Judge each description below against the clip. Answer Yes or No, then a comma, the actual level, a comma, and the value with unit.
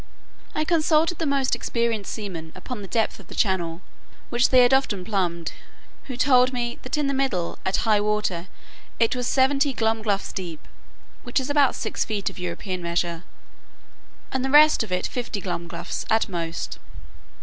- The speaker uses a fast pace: No, average, 170 wpm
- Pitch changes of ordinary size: No, wide, 6.3 semitones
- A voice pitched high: Yes, high, 225 Hz